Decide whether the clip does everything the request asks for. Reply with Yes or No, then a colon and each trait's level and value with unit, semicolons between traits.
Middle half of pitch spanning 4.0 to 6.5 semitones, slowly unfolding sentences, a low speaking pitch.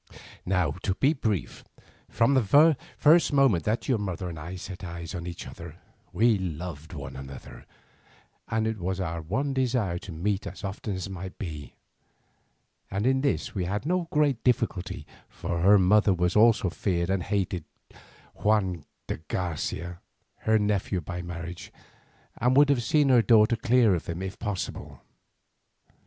No: average, 4.7 semitones; average, 155 wpm; very low, 95 Hz